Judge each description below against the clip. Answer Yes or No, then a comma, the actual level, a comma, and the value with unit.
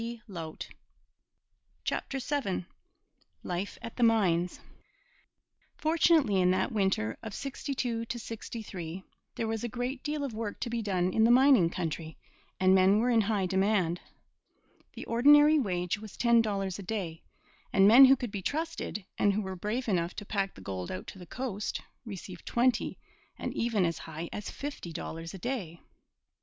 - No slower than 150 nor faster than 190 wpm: Yes, average, 160 wpm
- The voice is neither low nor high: No, high, 210 Hz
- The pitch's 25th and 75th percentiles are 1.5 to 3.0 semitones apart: No, average, 4.8 semitones